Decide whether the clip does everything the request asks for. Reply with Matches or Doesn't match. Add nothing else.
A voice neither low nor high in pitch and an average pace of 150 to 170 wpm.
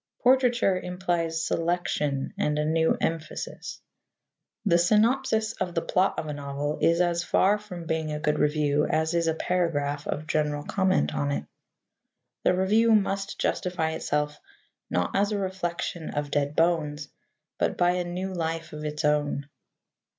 Matches